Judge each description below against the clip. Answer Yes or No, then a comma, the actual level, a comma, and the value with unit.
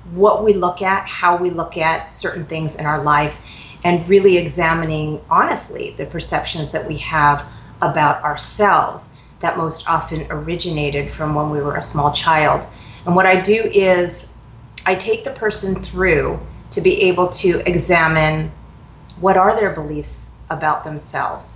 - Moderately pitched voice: Yes, medium, 165 Hz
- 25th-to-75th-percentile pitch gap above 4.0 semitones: No, average, 3.7 semitones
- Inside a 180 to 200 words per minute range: No, average, 155 wpm